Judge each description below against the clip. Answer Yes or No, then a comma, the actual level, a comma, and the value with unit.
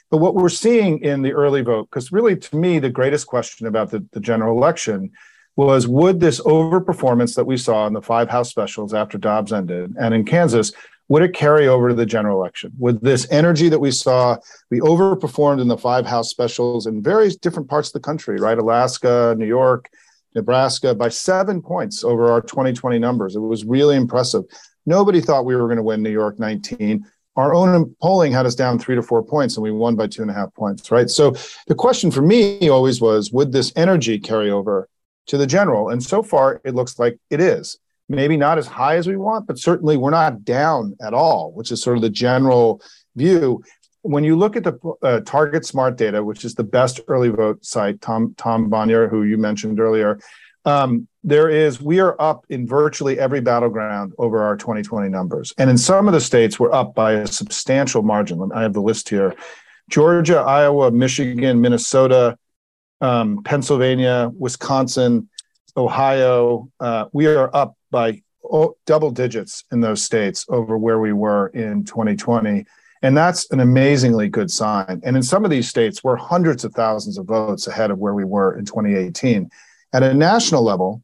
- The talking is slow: No, average, 195 wpm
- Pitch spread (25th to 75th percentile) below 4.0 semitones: No, average, 5.0 semitones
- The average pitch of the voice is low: Yes, low, 125 Hz